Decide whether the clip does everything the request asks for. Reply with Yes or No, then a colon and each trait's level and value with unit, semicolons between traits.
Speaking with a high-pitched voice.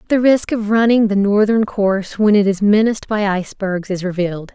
Yes: high, 205 Hz